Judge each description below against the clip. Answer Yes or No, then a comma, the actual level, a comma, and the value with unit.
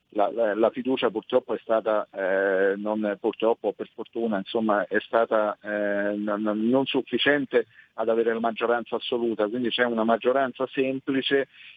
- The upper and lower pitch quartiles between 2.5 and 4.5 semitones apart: Yes, average, 3.3 semitones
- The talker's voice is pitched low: Yes, low, 115 Hz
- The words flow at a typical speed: Yes, average, 145 wpm